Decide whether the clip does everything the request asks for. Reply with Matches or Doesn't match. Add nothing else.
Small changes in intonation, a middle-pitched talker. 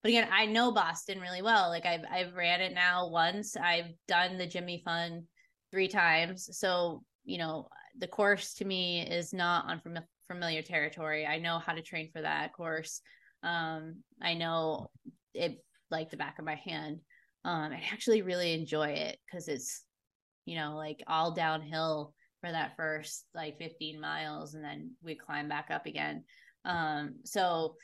Matches